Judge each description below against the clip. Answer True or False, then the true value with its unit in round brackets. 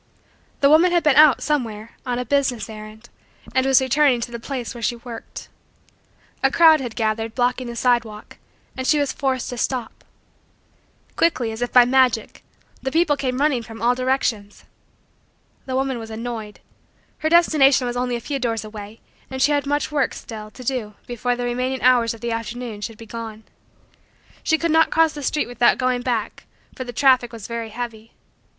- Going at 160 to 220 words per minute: True (185 wpm)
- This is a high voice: True (245 Hz)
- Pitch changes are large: False (2.9 semitones)